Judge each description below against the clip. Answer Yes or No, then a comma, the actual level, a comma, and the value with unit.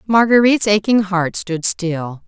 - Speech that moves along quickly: No, slow, 130 wpm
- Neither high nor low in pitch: No, high, 195 Hz